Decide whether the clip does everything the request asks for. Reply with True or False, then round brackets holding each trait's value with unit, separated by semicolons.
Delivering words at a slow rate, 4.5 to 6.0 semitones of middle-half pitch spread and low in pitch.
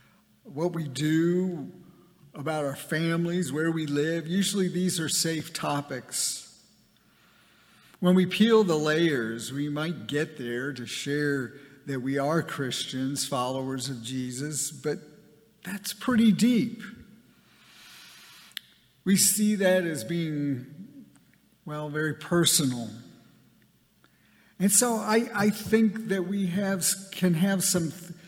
False (115 wpm; 5.2 semitones; 165 Hz)